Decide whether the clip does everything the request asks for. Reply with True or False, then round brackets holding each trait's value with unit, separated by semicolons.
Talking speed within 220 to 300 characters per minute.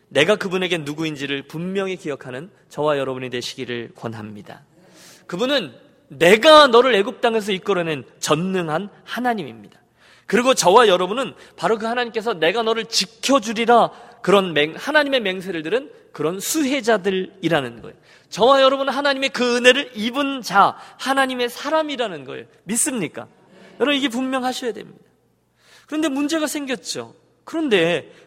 False (350 characters per minute)